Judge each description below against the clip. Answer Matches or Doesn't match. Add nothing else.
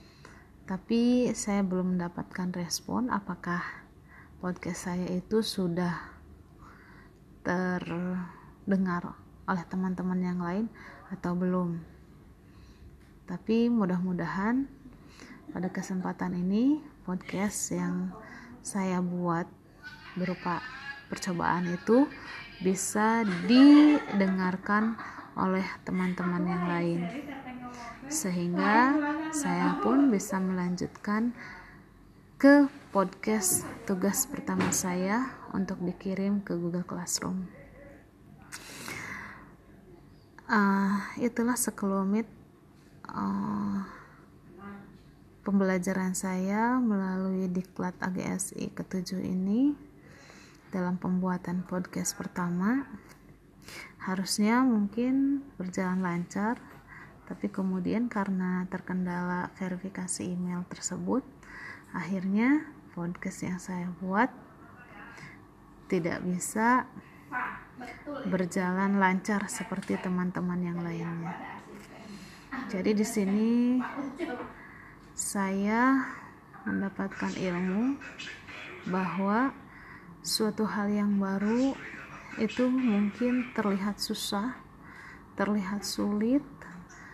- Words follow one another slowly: Matches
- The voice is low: Doesn't match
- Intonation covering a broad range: Doesn't match